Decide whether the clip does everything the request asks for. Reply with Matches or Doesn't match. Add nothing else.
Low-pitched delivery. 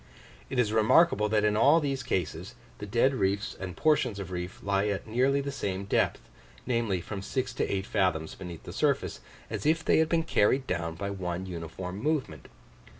Matches